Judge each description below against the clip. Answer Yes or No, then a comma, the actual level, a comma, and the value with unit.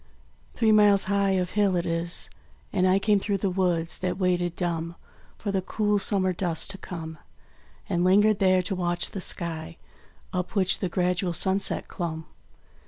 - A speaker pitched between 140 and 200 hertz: Yes, medium, 185 Hz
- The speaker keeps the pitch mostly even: Yes, narrow, 2.3 semitones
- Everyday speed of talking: Yes, average, 165 wpm